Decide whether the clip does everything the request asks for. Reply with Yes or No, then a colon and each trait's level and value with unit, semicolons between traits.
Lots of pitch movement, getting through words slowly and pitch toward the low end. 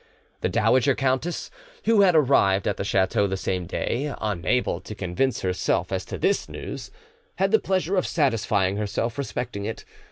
No: wide, 6.5 semitones; average, 170 wpm; low, 115 Hz